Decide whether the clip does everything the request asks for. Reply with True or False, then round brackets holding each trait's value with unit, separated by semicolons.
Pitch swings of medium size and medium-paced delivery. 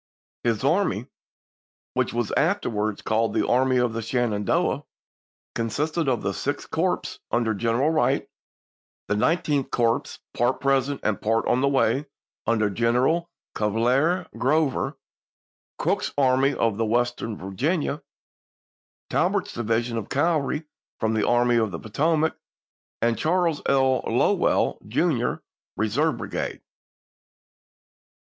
False (4.1 semitones; 120 wpm)